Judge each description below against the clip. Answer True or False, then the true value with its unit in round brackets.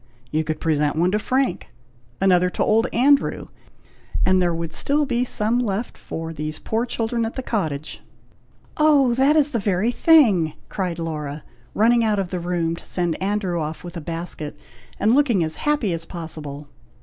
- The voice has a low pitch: False (185 Hz)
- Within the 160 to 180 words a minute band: True (175 wpm)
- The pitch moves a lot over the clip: True (6.4 semitones)